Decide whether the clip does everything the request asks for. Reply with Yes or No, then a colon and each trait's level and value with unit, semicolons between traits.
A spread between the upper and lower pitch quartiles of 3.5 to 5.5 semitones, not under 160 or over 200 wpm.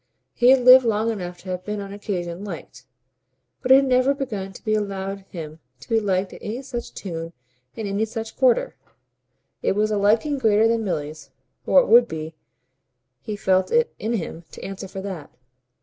Yes: average, 3.9 semitones; average, 195 wpm